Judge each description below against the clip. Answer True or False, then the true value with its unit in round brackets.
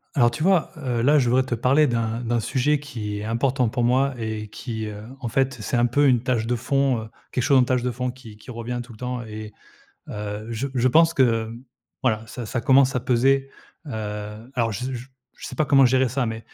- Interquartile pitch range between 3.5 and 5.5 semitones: False (2.8 semitones)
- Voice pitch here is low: True (125 Hz)